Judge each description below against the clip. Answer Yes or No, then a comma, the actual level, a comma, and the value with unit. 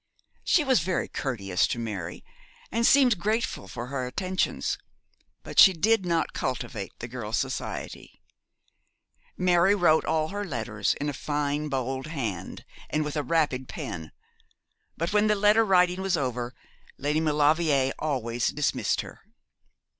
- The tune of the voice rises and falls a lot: Yes, wide, 6.3 semitones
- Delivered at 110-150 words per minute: Yes, average, 140 wpm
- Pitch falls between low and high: Yes, medium, 150 Hz